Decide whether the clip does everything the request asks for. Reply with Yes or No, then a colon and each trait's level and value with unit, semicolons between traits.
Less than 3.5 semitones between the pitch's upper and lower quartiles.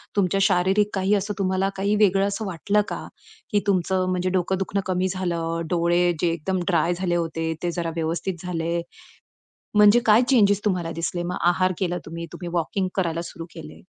Yes: narrow, 2.4 semitones